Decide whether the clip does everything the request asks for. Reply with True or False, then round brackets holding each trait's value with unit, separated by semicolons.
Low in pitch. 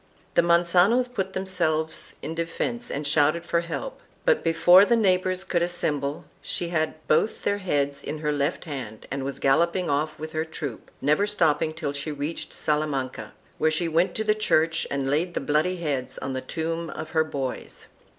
False (160 Hz)